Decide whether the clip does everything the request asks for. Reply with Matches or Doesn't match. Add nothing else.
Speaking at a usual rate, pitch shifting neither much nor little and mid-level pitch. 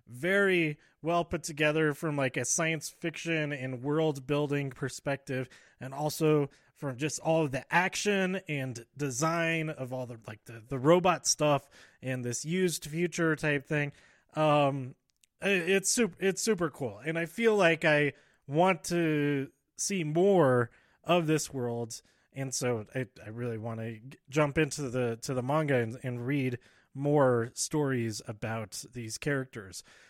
Matches